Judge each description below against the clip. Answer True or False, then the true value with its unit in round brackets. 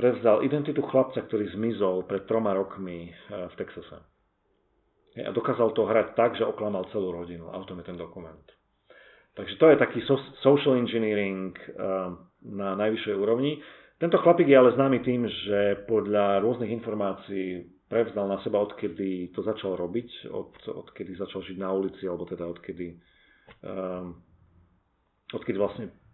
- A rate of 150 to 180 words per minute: False (140 wpm)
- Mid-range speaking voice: False (100 Hz)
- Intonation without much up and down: False (4.1 semitones)